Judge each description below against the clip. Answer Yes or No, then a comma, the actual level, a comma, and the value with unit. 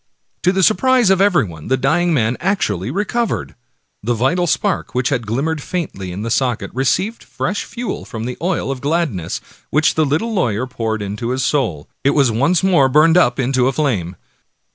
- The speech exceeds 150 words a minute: Yes, average, 180 wpm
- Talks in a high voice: No, low, 135 Hz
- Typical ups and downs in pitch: No, wide, 7.1 semitones